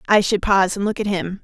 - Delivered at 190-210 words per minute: No, fast, 290 wpm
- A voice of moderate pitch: No, high, 195 Hz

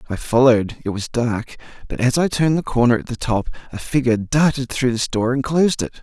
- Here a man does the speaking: Yes, male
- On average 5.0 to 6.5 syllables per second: Yes, 6.1 syllables/s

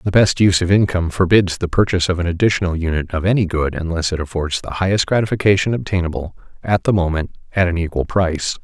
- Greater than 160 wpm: Yes, average, 200 wpm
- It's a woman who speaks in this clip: No, male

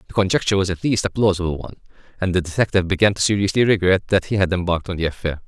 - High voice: No, very low, 95 Hz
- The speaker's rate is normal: No, fast, 240 wpm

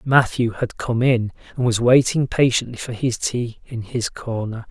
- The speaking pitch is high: No, low, 120 Hz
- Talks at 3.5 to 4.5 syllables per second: Yes, 4.4 syllables/s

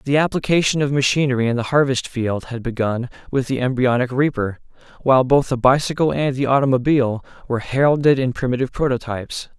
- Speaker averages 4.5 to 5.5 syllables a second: No, 6.2 syllables/s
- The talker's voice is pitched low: Yes, low, 130 Hz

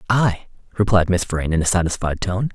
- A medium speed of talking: Yes, average, 190 wpm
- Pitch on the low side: Yes, very low, 95 Hz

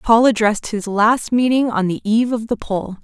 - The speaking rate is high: Yes, fast, 215 wpm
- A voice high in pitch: Yes, high, 225 Hz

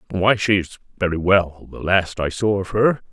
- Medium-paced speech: Yes, average, 190 wpm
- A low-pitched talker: Yes, very low, 95 Hz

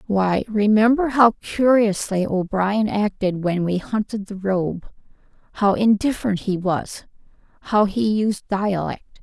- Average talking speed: No, slow, 110 wpm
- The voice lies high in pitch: Yes, high, 205 Hz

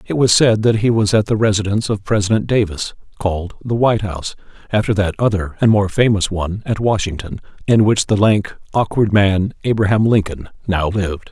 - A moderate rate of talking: Yes, average, 185 wpm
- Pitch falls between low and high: No, low, 105 Hz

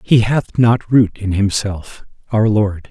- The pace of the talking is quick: No, average, 145 wpm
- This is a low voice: Yes, low, 105 Hz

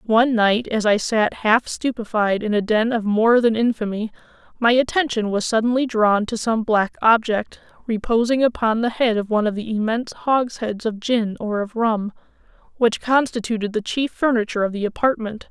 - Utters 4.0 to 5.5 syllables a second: Yes, 5.1 syllables/s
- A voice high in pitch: Yes, high, 225 Hz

